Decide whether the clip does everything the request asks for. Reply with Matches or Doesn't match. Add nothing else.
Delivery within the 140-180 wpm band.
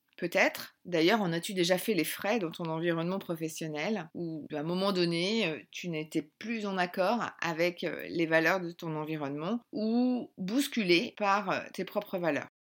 Matches